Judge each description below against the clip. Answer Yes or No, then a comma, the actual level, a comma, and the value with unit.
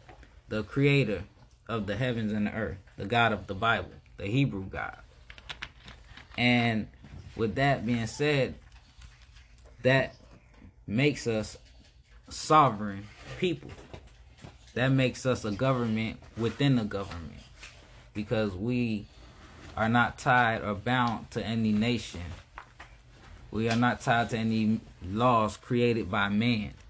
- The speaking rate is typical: No, slow, 120 wpm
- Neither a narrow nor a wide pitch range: Yes, average, 3.4 semitones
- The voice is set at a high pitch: No, low, 110 Hz